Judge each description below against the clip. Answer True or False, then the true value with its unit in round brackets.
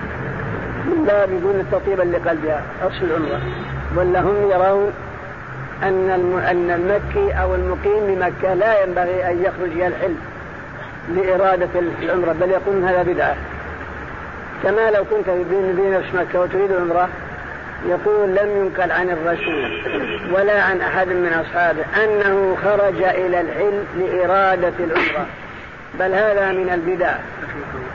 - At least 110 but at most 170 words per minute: True (115 wpm)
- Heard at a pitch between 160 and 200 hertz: True (185 Hz)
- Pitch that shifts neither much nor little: False (1.7 semitones)